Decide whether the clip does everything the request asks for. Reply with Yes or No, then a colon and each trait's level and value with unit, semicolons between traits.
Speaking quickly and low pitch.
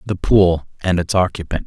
No: average, 145 wpm; very low, 90 Hz